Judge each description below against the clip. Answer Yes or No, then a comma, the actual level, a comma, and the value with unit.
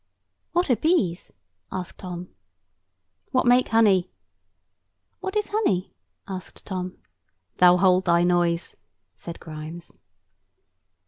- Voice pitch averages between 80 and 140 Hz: No, medium, 185 Hz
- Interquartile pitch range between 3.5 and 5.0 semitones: Yes, average, 4.6 semitones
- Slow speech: Yes, slow, 105 wpm